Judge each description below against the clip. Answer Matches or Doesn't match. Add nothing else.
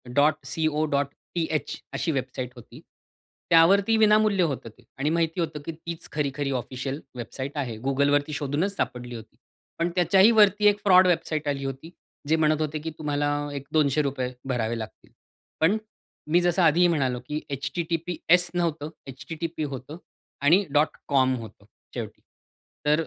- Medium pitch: Matches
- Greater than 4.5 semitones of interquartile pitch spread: Doesn't match